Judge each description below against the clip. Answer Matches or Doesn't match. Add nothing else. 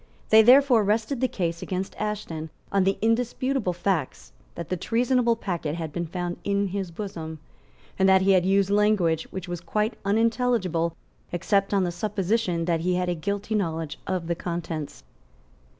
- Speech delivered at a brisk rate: Doesn't match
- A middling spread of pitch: Matches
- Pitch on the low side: Doesn't match